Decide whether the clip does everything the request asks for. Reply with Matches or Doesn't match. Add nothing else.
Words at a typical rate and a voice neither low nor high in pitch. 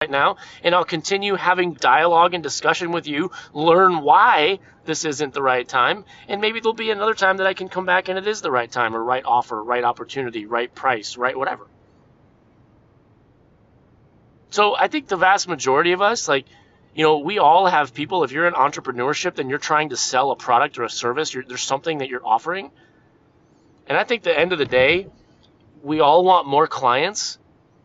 Matches